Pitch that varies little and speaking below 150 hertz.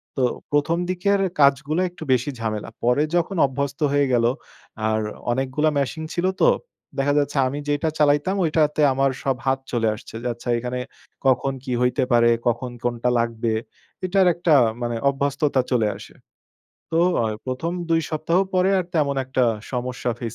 No: average, 3.9 semitones; medium, 140 Hz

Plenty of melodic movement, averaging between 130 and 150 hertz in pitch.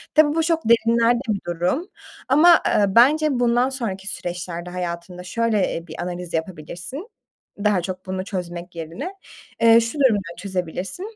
No: wide, 5.7 semitones; high, 195 Hz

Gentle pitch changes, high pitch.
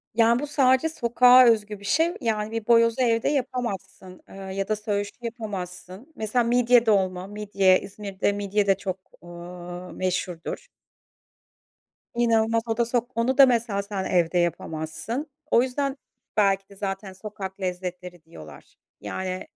No: average, 3.8 semitones; high, 210 Hz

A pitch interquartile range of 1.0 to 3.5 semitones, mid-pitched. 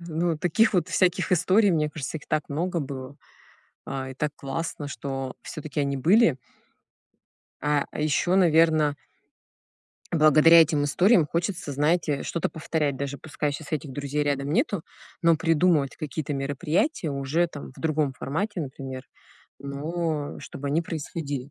Yes: average, 3.0 semitones; medium, 150 Hz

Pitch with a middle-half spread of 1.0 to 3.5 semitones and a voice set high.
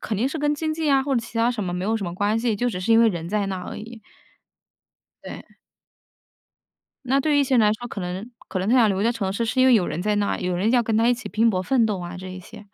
No: average, 4.0 semitones; high, 220 Hz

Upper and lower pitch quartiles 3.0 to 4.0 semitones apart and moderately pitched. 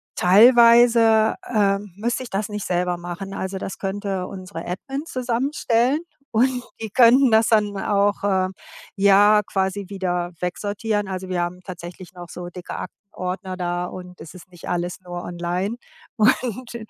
No: average, 3.7 semitones; high, 195 Hz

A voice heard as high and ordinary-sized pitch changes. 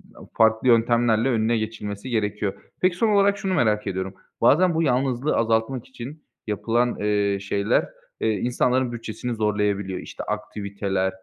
No: low, 110 Hz; average, 3.3 semitones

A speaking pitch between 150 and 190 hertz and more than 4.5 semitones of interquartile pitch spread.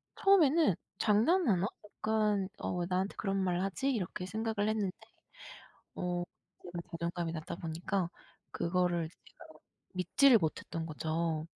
No: medium, 185 Hz; average, 4.1 semitones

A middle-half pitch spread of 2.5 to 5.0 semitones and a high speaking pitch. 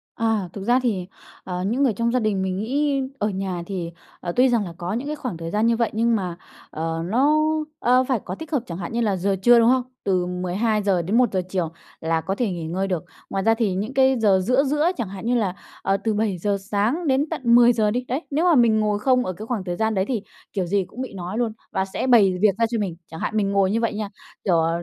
Yes: average, 4.4 semitones; high, 210 Hz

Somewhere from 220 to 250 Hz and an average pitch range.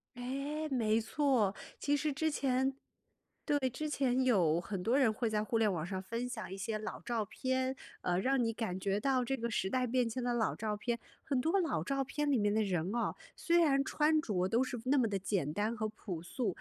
Yes: high, 235 Hz; average, 4.4 semitones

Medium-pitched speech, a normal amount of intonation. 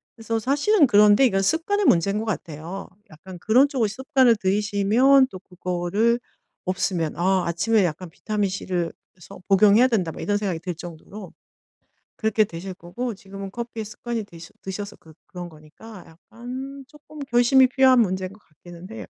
No: high, 205 Hz; average, 4.8 semitones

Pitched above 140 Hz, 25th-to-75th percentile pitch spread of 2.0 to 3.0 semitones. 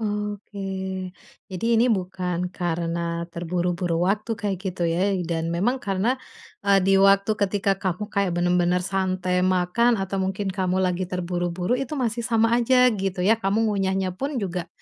Yes: high, 190 Hz; narrow, 2.6 semitones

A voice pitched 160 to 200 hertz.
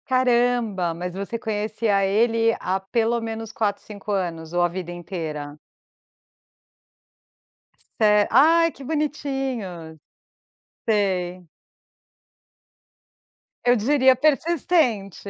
No: high, 215 Hz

